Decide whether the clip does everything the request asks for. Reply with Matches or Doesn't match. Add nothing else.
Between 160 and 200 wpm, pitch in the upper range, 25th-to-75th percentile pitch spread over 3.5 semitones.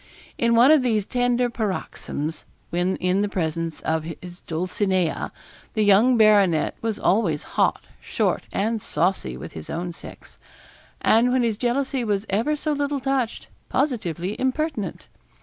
Doesn't match